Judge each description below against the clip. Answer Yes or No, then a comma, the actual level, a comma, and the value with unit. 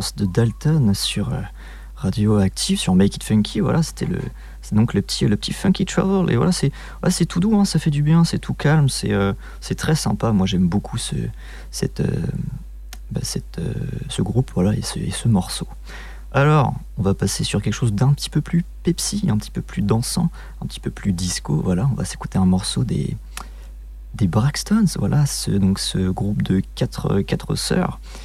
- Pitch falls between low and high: No, low, 115 Hz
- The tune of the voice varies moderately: No, wide, 8.8 semitones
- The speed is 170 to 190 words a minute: No, average, 210 wpm